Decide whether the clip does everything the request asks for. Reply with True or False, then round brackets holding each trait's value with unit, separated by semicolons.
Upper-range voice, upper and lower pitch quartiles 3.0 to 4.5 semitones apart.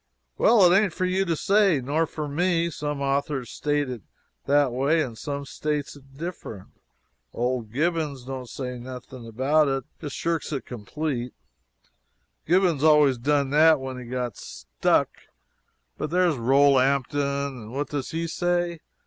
False (140 Hz; 3.8 semitones)